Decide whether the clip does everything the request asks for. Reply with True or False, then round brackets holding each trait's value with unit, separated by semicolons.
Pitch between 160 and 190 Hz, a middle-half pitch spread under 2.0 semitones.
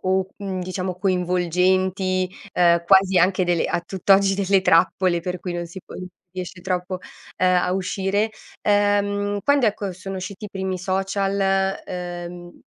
True (185 Hz; 1.4 semitones)